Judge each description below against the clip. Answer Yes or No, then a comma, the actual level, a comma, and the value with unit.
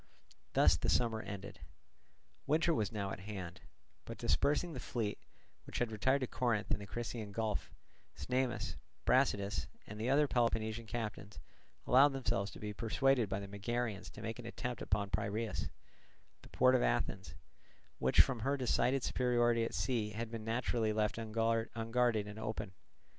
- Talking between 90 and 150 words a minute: No, average, 160 wpm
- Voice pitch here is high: No, low, 115 Hz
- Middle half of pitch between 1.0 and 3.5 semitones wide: Yes, average, 2.9 semitones